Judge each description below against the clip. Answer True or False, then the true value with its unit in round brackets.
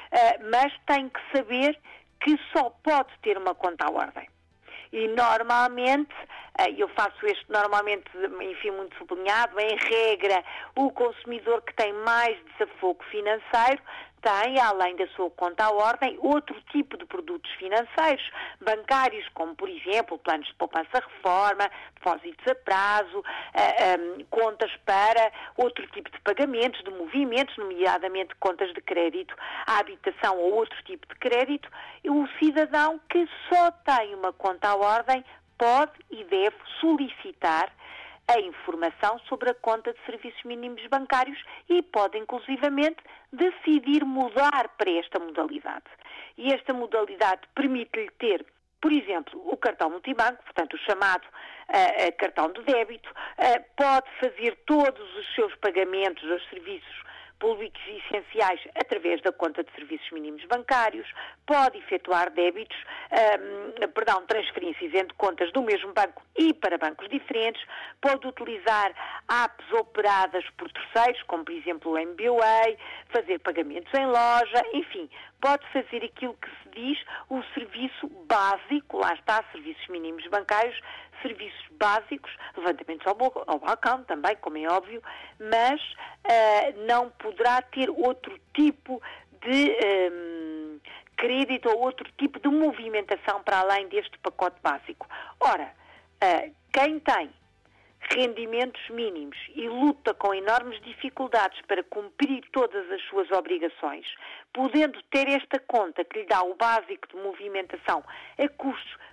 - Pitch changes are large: True (6.4 semitones)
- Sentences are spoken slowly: False (135 wpm)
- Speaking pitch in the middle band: False (245 Hz)